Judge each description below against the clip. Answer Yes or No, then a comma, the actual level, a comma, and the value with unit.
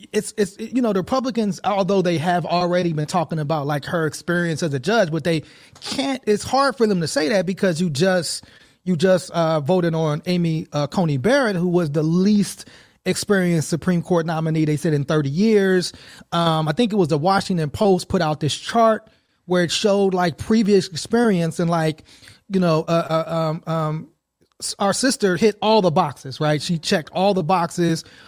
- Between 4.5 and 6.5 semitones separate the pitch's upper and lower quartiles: No, average, 3.7 semitones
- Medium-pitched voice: Yes, medium, 180 Hz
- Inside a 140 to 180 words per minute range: No, average, 195 wpm